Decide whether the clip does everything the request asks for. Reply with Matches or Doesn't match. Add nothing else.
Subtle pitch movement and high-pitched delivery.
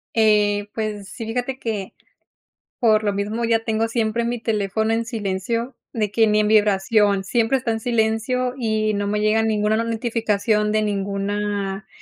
Matches